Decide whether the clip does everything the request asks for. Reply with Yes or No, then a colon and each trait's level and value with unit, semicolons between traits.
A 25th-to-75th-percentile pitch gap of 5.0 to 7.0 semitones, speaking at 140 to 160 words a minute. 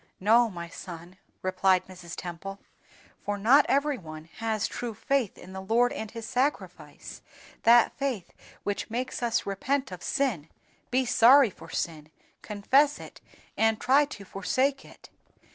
Yes: wide, 5.5 semitones; average, 145 wpm